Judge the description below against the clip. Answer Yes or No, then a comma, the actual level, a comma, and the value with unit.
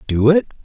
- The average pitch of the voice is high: No, medium, 145 Hz